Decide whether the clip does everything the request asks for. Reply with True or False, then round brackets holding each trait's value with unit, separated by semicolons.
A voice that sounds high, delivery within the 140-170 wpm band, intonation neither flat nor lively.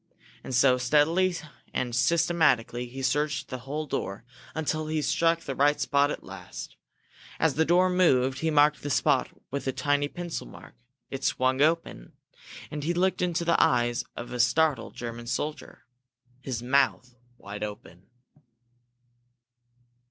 False (140 Hz; 145 wpm; 4.4 semitones)